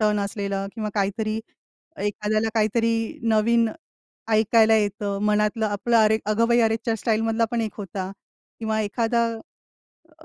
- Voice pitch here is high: Yes, high, 220 Hz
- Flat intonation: Yes, narrow, 1.4 semitones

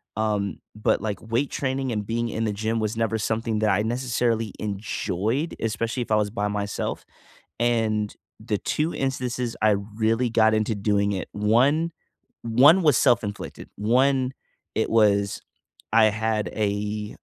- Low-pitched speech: Yes, low, 110 Hz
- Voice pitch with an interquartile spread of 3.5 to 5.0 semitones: No, narrow, 2.4 semitones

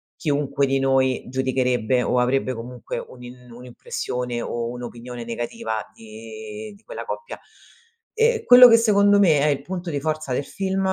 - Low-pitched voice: Yes, low, 130 Hz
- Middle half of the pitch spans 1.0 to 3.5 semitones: No, wide, 5.9 semitones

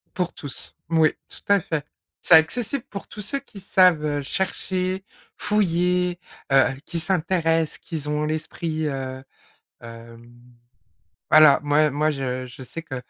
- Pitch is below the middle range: No, medium, 160 Hz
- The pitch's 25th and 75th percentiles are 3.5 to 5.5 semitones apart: Yes, average, 4.2 semitones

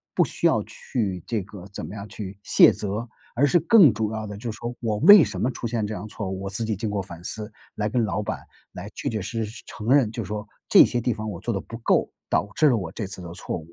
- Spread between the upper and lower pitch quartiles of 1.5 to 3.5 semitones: Yes, average, 2.8 semitones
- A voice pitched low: Yes, low, 105 Hz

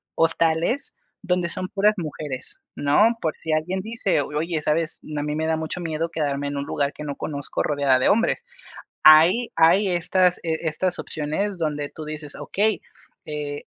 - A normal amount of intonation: Yes, average, 3.5 semitones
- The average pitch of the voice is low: No, medium, 160 Hz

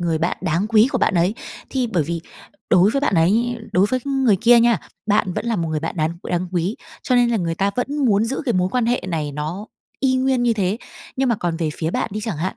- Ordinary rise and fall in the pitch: No, wide, 5.9 semitones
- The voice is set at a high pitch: Yes, high, 205 Hz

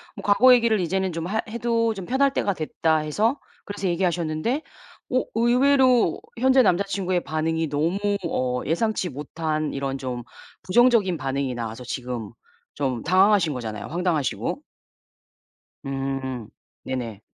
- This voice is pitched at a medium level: Yes, medium, 170 Hz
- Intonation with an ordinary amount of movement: No, wide, 8.1 semitones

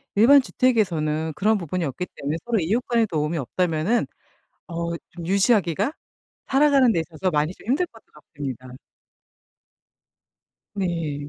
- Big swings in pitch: Yes, wide, 6.3 semitones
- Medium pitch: Yes, medium, 175 Hz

